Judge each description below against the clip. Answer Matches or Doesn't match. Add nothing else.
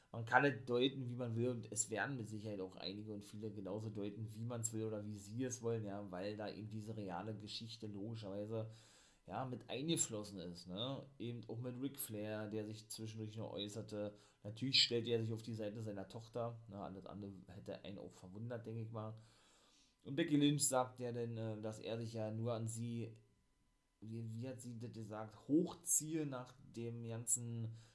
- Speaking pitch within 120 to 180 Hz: Doesn't match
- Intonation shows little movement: Matches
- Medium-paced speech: Doesn't match